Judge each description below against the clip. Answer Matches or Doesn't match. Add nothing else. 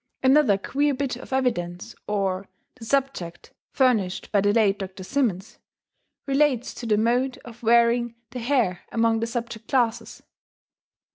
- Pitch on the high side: Matches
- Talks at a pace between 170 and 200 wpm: Doesn't match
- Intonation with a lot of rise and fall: Doesn't match